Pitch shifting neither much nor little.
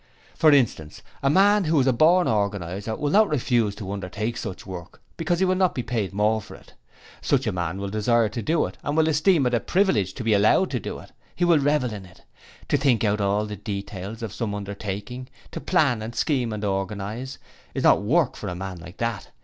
No: wide, 6.3 semitones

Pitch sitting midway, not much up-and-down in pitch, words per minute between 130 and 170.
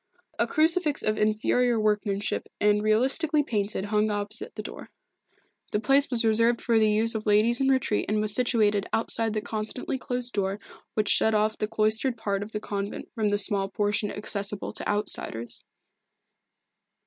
No: high, 215 Hz; narrow, 2.2 semitones; average, 165 wpm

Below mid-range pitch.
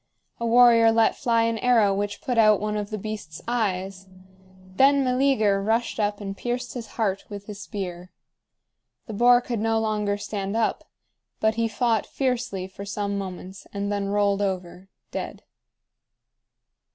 No: high, 210 Hz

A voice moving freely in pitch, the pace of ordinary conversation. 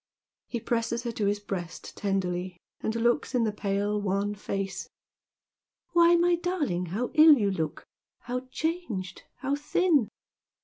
Yes: wide, 6.1 semitones; average, 150 wpm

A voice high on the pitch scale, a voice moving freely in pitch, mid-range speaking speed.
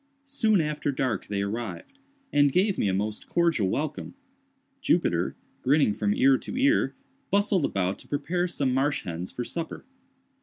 No: medium, 140 Hz; wide, 8.9 semitones; average, 155 wpm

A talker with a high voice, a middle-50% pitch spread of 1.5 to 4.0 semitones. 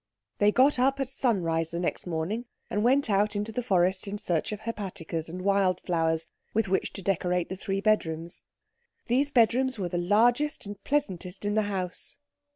No: high, 200 Hz; average, 4.4 semitones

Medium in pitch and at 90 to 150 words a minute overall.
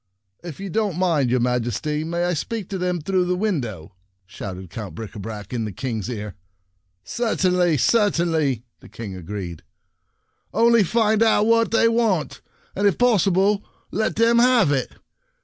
No: medium, 170 Hz; average, 165 wpm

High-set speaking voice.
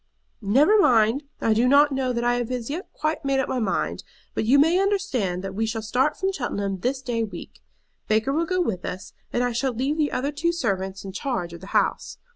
Yes: very high, 250 Hz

